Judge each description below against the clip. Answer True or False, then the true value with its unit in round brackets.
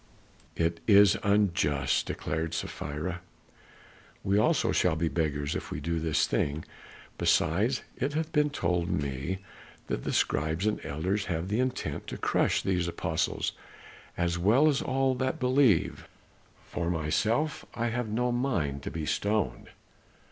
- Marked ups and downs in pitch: True (7.0 semitones)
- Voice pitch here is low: True (90 Hz)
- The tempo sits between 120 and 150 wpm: True (140 wpm)